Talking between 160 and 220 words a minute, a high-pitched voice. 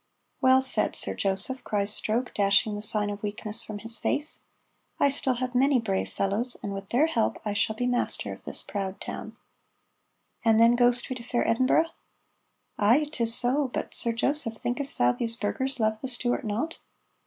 Yes: average, 185 wpm; high, 235 Hz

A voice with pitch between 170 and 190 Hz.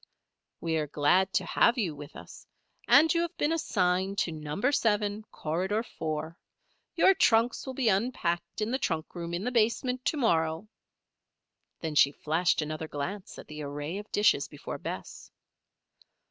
Yes: medium, 185 Hz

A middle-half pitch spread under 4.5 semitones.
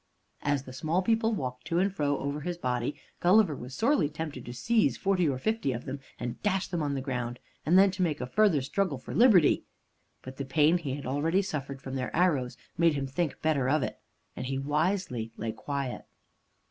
No: wide, 5.4 semitones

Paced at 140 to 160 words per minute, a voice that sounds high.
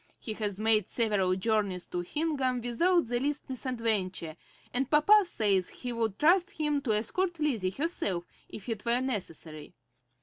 Yes: average, 155 wpm; high, 230 Hz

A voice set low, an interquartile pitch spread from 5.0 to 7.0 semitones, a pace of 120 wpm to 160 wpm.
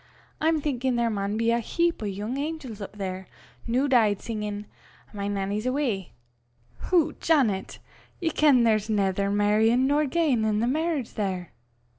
No: high, 225 Hz; wide, 5.4 semitones; average, 150 wpm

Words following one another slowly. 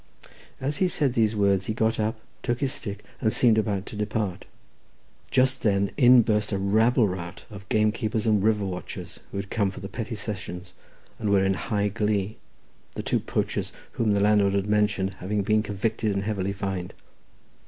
No: average, 185 wpm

